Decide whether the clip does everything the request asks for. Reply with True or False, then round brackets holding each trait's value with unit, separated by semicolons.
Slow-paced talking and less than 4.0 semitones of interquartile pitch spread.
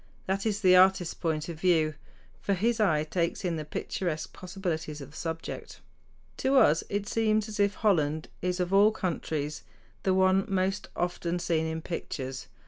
False (170 wpm; 3.6 semitones)